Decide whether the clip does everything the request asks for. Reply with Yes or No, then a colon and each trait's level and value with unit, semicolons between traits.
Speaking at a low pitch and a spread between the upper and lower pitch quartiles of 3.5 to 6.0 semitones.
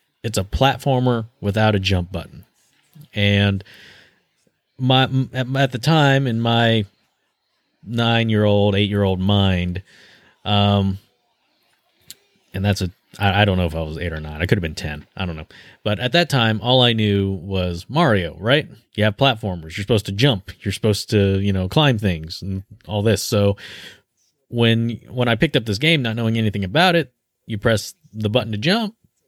Yes: low, 105 Hz; average, 4.3 semitones